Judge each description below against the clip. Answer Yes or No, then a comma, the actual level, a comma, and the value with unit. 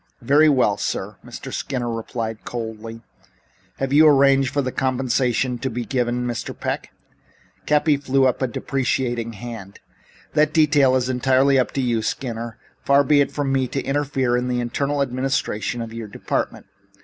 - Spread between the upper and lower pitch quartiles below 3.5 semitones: Yes, narrow, 2.5 semitones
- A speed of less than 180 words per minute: Yes, average, 160 wpm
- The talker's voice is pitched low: Yes, low, 130 Hz